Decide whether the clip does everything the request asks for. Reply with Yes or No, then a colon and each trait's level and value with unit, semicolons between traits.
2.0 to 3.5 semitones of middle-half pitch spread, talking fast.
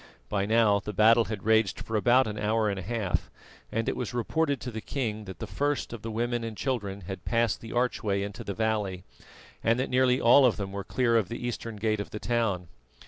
Yes: average, 2.8 semitones; fast, 230 wpm